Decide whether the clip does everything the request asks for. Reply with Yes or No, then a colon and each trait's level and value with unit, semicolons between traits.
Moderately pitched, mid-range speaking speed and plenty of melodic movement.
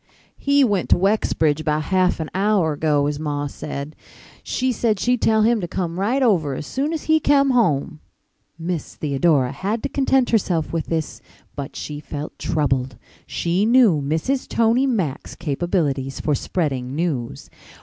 Yes: medium, 170 Hz; average, 160 wpm; wide, 7.2 semitones